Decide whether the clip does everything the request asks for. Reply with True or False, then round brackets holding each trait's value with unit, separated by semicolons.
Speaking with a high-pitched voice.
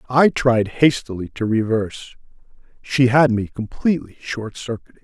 False (120 Hz)